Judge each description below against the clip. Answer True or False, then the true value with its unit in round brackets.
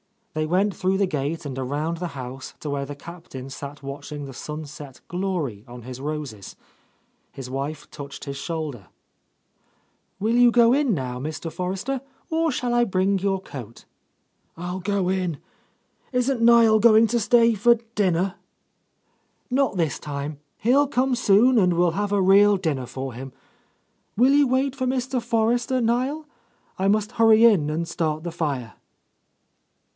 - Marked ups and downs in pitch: True (8.1 semitones)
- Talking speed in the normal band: True (160 wpm)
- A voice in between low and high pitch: True (180 Hz)